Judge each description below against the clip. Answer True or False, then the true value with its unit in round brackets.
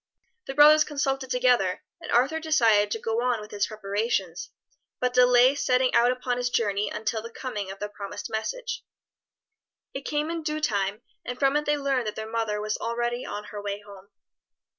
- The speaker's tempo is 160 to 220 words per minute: True (185 wpm)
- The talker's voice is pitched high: True (240 Hz)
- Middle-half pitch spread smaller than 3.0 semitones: False (4.4 semitones)